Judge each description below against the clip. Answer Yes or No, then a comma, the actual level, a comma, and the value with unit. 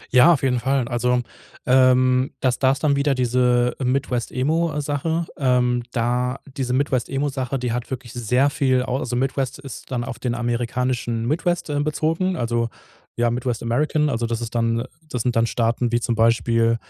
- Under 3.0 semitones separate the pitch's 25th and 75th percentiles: Yes, narrow, 2.4 semitones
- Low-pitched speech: Yes, low, 125 Hz